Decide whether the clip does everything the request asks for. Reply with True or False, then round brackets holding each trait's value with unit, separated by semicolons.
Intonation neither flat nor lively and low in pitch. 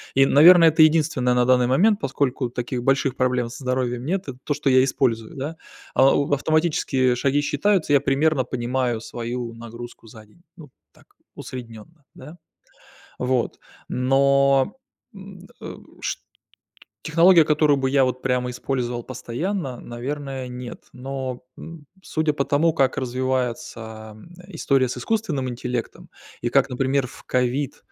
True (3.0 semitones; 130 Hz)